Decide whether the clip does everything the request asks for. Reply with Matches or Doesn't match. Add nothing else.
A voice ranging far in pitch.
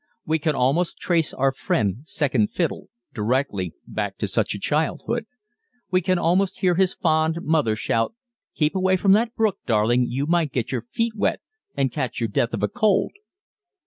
Matches